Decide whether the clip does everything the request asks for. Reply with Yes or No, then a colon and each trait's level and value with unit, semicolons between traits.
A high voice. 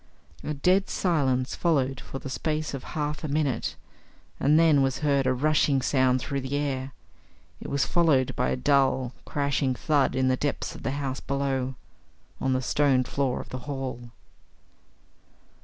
No: low, 135 Hz